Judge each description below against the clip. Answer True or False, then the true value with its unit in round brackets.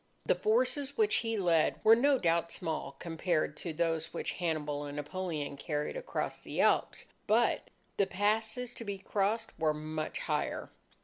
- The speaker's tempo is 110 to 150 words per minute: False (160 wpm)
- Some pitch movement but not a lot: False (6.2 semitones)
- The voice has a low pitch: False (175 Hz)